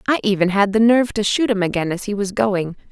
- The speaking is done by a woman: Yes, female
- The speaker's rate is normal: No, fast, 265 wpm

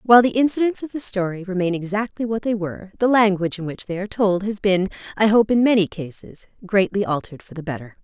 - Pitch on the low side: No, high, 200 Hz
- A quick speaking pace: Yes, fast, 225 wpm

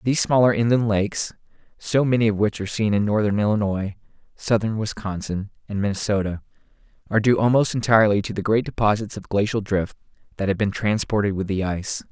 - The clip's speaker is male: Yes, male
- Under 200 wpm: Yes, average, 175 wpm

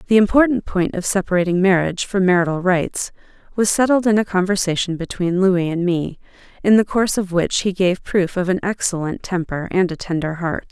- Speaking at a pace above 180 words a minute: Yes, average, 190 wpm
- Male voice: No, female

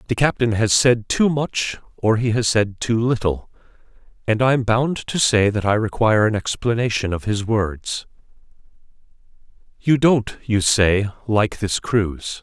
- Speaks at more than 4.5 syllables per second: No, 4.3 syllables/s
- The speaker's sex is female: No, male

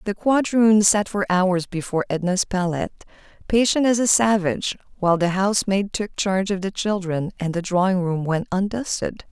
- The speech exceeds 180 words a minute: No, average, 175 wpm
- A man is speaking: No, female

